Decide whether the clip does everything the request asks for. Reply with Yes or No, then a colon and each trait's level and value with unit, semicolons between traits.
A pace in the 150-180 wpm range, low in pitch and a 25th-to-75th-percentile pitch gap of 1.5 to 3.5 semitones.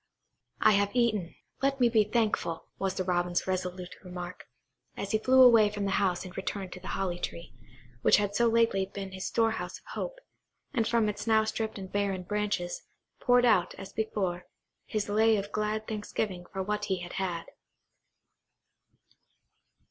No: average, 170 wpm; high, 205 Hz; average, 2.9 semitones